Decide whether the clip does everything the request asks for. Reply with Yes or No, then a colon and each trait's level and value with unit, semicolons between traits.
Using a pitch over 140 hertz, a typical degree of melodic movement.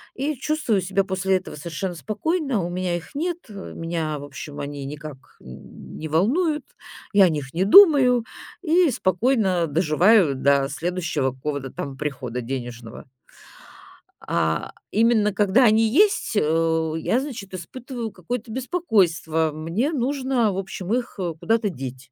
No: medium, 185 Hz; wide, 7.7 semitones